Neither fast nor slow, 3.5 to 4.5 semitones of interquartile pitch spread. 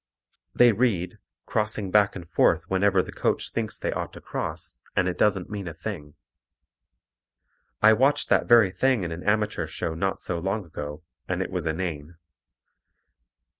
Yes: average, 165 wpm; average, 3.8 semitones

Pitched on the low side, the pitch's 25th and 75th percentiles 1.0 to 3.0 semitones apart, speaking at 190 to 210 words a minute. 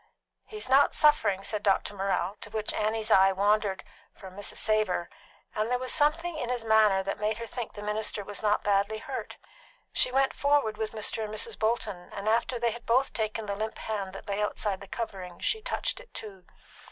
No: high, 215 Hz; average, 2.7 semitones; average, 200 wpm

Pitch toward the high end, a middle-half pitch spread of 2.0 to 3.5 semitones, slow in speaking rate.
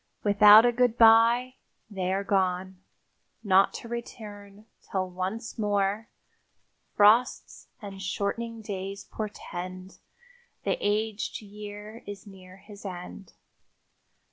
Yes: high, 205 Hz; narrow, 2.4 semitones; slow, 100 wpm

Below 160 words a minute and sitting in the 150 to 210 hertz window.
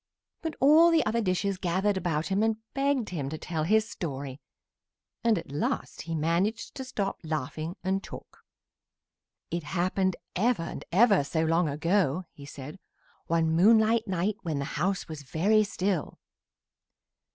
Yes: average, 150 wpm; medium, 185 Hz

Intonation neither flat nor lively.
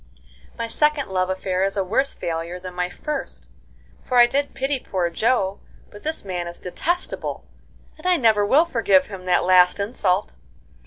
No: wide, 6.5 semitones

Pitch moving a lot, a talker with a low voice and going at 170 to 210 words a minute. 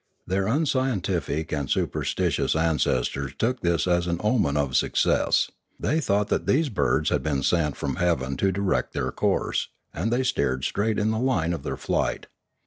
Yes: wide, 7.1 semitones; very low, 90 Hz; average, 175 wpm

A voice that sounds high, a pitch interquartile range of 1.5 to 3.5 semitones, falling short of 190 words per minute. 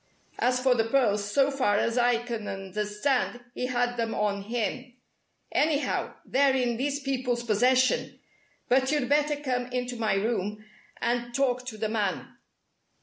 Yes: high, 245 Hz; average, 3.0 semitones; average, 150 wpm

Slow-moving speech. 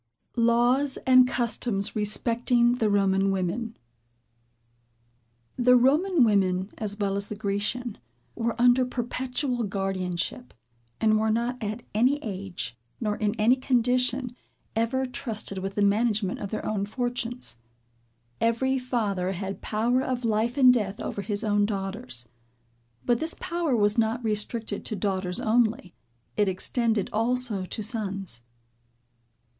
Yes: slow, 130 wpm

